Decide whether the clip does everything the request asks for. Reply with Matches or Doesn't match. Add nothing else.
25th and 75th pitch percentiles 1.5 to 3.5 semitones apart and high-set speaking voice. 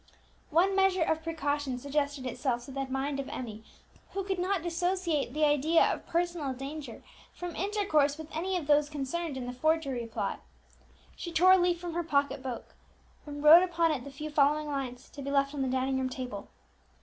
Doesn't match